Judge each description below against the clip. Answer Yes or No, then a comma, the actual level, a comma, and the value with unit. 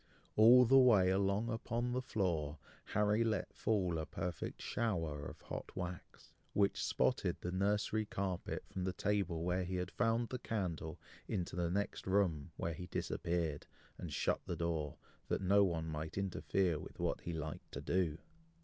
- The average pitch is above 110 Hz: No, very low, 95 Hz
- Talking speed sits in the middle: Yes, average, 165 wpm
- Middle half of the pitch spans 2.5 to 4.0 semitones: Yes, average, 3.7 semitones